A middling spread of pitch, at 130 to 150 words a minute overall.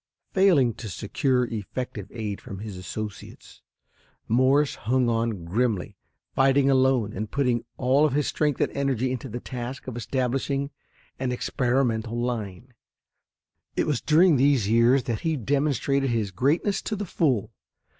Yes: average, 3.4 semitones; average, 145 wpm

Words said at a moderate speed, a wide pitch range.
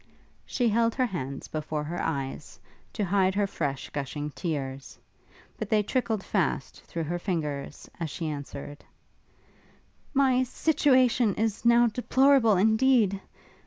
No: slow, 125 wpm; wide, 8.0 semitones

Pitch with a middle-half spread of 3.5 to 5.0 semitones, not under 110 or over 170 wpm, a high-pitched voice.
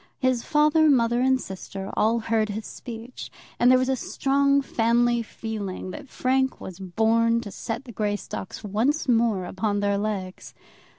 Yes: average, 3.9 semitones; average, 160 wpm; high, 230 Hz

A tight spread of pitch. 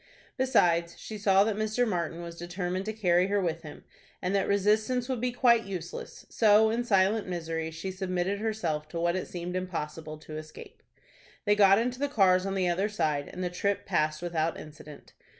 No: average, 3.9 semitones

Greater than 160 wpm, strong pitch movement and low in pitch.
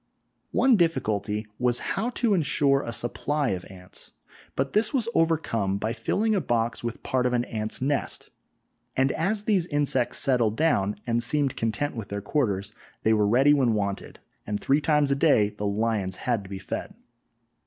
Yes: average, 175 wpm; wide, 5.7 semitones; low, 125 Hz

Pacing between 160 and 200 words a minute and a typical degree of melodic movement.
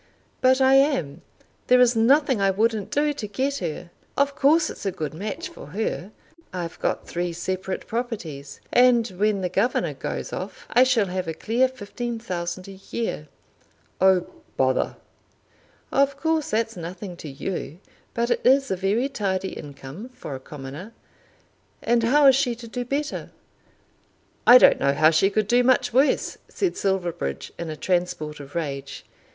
No: average, 165 wpm; wide, 6.5 semitones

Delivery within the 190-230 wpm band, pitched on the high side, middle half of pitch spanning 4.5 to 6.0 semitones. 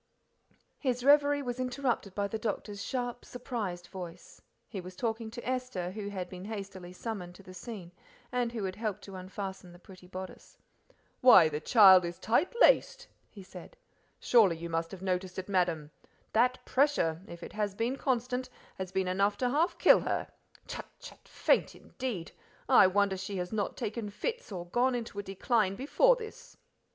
No: average, 175 wpm; high, 205 Hz; average, 5.0 semitones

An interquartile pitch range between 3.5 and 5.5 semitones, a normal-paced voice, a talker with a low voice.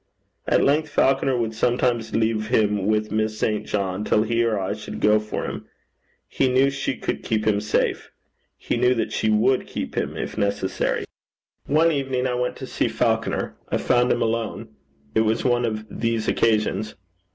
No: narrow, 2.5 semitones; average, 185 wpm; low, 115 Hz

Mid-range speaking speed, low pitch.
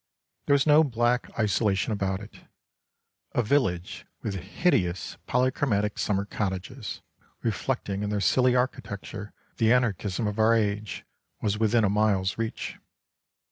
No: slow, 130 wpm; low, 105 Hz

